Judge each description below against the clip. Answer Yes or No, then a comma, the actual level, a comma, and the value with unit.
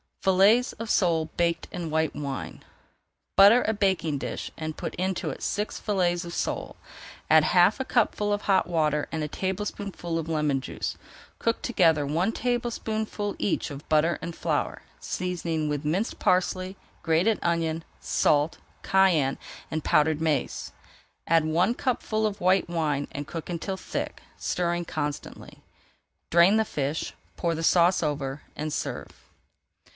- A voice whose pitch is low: No, medium, 170 Hz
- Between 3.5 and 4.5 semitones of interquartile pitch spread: Yes, average, 3.8 semitones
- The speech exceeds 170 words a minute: No, average, 145 wpm